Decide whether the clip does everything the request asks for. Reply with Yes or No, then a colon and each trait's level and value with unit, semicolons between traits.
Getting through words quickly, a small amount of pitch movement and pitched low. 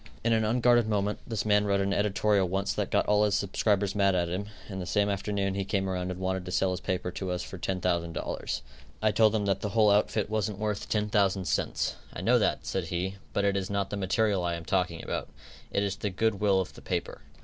Yes: fast, 245 wpm; narrow, 1.9 semitones; low, 100 Hz